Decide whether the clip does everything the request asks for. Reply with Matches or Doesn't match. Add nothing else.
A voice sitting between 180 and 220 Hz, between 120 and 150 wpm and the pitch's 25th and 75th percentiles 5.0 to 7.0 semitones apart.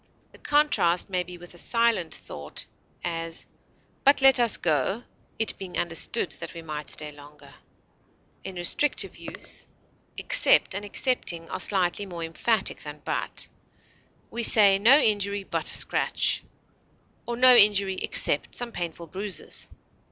Matches